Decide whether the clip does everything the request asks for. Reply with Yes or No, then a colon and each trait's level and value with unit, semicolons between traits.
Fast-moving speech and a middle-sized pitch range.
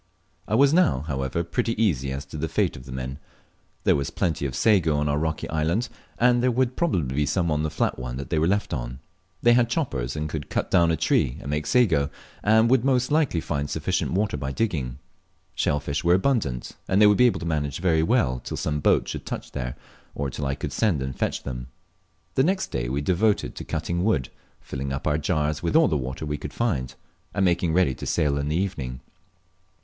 No: fast, 225 wpm; wide, 7.1 semitones